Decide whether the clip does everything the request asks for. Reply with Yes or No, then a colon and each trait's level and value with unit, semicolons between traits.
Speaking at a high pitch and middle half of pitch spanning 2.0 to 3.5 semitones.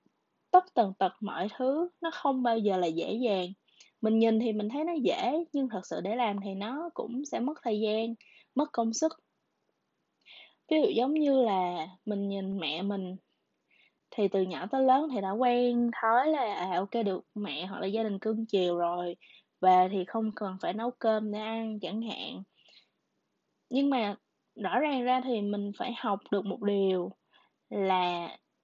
No: high, 220 Hz; average, 4.4 semitones